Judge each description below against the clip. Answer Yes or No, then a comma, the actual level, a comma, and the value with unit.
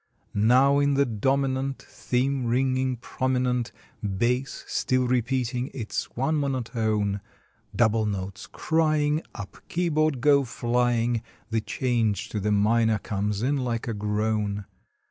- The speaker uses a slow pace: Yes, slow, 120 wpm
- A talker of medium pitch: No, low, 120 Hz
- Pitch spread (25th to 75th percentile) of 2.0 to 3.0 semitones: No, average, 3.7 semitones